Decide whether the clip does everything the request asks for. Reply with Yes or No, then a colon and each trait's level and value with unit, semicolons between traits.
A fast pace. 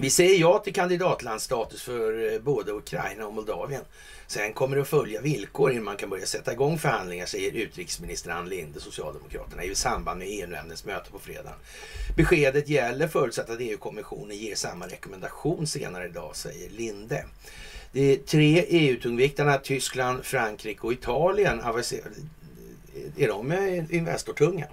No: average, 140 wpm